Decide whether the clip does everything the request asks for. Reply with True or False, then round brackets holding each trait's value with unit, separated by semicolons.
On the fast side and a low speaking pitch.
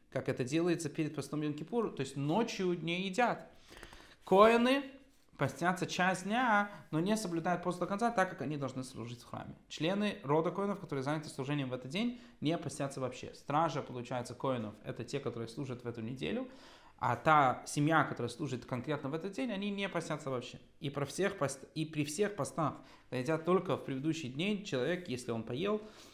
False (185 wpm; 155 Hz)